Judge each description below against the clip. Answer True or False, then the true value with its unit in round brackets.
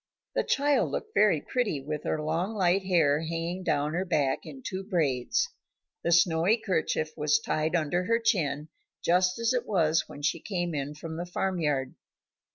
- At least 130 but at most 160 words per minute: False (175 wpm)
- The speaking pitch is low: False (170 Hz)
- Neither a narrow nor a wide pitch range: True (4.0 semitones)